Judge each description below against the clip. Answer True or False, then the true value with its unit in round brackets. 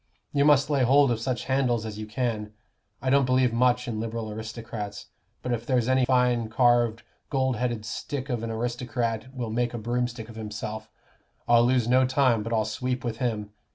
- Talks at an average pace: True (190 wpm)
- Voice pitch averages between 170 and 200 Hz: False (120 Hz)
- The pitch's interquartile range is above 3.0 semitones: False (2.4 semitones)